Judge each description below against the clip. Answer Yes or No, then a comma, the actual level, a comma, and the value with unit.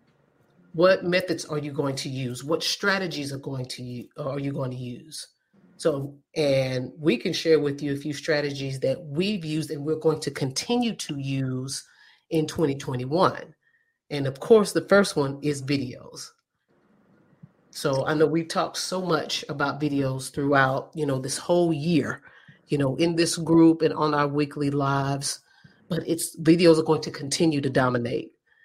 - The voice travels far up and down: No, average, 3.2 semitones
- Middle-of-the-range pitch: Yes, medium, 150 Hz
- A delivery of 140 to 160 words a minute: No, average, 170 wpm